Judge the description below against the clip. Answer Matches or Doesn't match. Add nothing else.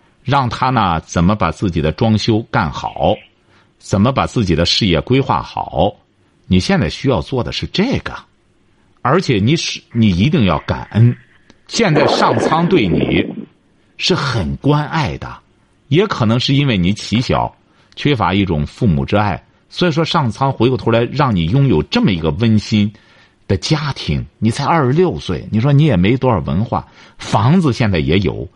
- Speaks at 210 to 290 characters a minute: Matches